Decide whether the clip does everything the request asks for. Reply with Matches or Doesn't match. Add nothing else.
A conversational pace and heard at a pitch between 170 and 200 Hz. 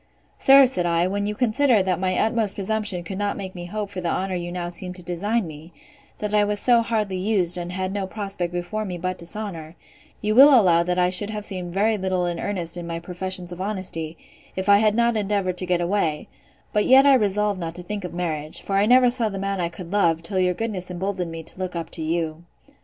Doesn't match